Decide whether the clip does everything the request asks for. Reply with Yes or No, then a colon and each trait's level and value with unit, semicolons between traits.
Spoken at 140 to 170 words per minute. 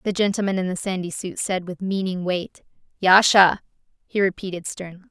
Yes: average, 165 wpm